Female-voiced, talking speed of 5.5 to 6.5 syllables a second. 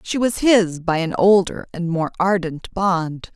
No: female; 3.9 syllables/s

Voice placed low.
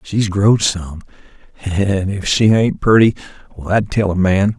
Yes: low, 100 Hz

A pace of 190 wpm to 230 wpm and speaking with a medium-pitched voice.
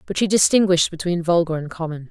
Yes: average, 200 wpm; medium, 170 Hz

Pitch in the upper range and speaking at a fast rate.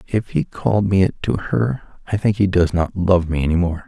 No: very low, 95 Hz; fast, 265 wpm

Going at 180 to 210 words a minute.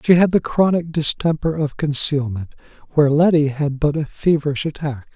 No: average, 165 wpm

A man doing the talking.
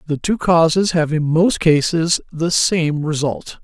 Yes: male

